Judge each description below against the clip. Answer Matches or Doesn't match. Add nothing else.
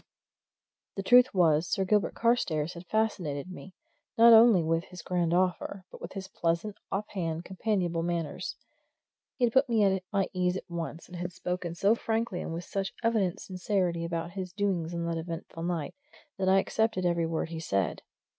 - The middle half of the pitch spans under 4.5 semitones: Matches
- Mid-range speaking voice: Matches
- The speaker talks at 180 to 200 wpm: Matches